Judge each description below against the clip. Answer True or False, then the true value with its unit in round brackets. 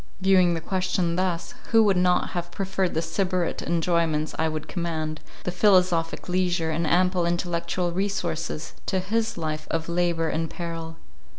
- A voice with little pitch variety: True (2.0 semitones)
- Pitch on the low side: False (175 Hz)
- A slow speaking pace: False (155 wpm)